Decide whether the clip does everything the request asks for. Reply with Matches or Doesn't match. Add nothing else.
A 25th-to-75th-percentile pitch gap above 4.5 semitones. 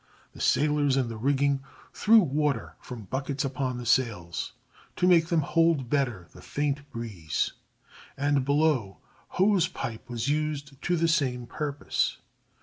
Doesn't match